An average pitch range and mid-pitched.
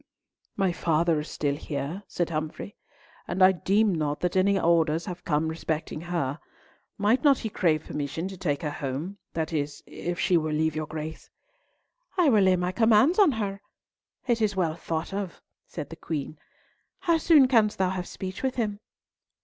Yes: average, 4.5 semitones; medium, 175 Hz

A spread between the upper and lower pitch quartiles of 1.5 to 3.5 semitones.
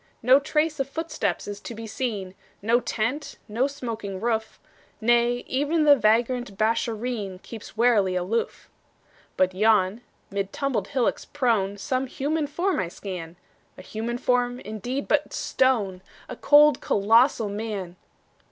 No: average, 4.4 semitones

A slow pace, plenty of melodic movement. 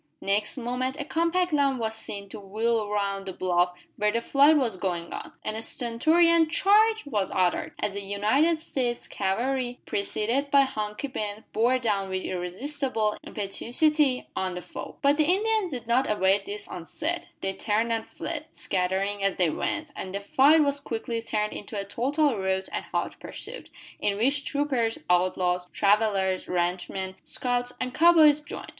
No: average, 170 wpm; wide, 6.2 semitones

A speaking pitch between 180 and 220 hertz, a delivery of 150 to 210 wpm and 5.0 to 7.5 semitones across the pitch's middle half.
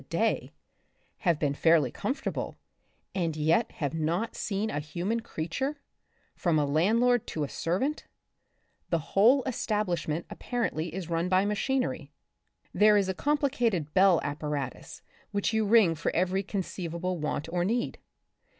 No: medium, 185 Hz; average, 140 wpm; wide, 5.4 semitones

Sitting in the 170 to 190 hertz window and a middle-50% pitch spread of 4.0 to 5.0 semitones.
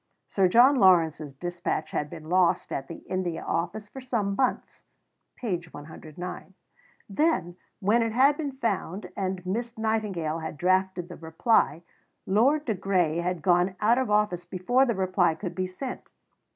Yes: medium, 185 Hz; average, 4.4 semitones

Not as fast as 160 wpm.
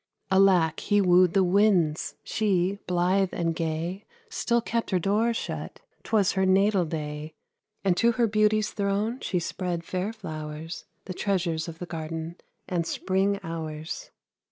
Yes: average, 145 wpm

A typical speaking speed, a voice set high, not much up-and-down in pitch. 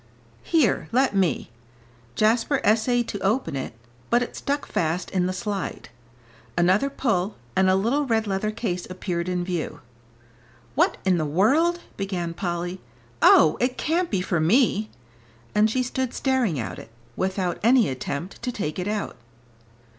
No: average, 155 wpm; high, 195 Hz; wide, 5.4 semitones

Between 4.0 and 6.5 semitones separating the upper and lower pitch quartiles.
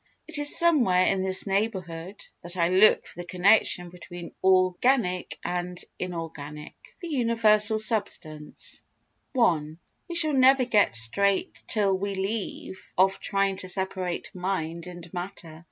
No: average, 3.4 semitones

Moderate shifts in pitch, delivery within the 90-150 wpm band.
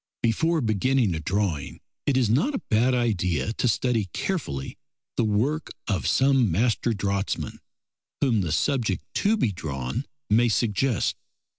Yes: average, 4.9 semitones; average, 140 wpm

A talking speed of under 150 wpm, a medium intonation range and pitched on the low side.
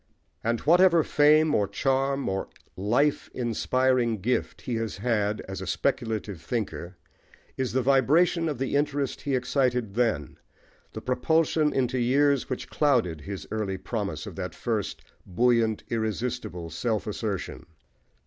Yes: slow, 135 wpm; average, 4.7 semitones; low, 120 Hz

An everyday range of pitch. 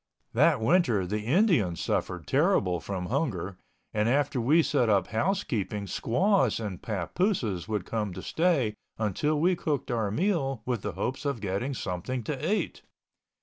No: wide, 7.0 semitones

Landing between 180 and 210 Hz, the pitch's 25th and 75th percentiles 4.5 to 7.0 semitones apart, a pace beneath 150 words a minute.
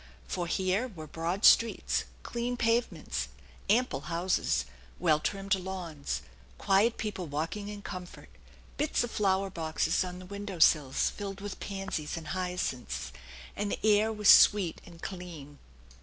No: high, 190 Hz; average, 3.7 semitones; average, 140 wpm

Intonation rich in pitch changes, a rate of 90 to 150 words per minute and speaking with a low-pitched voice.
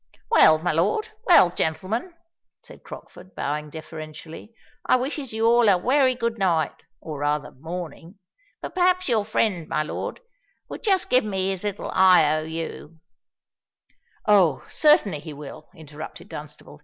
No: wide, 6.9 semitones; average, 140 wpm; medium, 180 Hz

